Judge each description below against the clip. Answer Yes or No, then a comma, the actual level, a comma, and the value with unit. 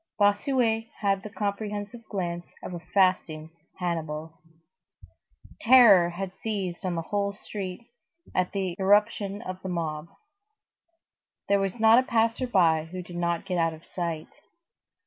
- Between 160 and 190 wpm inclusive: No, average, 140 wpm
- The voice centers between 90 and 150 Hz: No, high, 190 Hz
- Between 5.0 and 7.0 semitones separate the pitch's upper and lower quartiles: No, average, 3.3 semitones